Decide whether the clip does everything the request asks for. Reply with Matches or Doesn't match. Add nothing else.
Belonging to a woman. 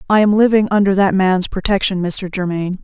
Matches